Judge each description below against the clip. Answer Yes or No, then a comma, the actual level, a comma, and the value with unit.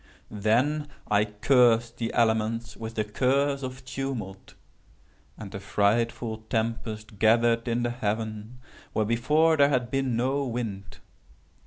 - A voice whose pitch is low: Yes, low, 115 Hz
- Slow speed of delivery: Yes, slow, 130 wpm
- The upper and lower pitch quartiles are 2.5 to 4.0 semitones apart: Yes, average, 2.9 semitones